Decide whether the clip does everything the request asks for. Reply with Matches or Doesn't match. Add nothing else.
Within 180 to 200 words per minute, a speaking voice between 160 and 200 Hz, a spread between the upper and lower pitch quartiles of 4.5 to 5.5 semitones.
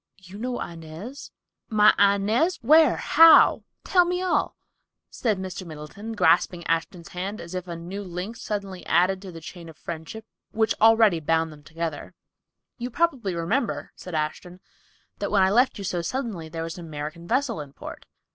Doesn't match